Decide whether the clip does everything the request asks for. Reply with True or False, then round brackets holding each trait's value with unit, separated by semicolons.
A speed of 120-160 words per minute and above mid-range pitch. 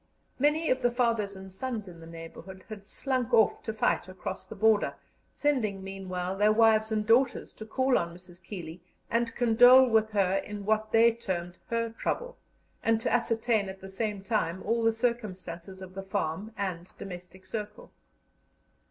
False (170 wpm; 210 Hz)